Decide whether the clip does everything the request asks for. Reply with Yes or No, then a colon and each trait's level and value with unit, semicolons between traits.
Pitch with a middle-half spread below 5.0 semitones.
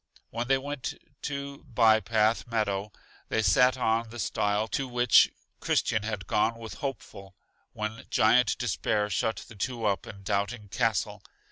Yes: narrow, 2.6 semitones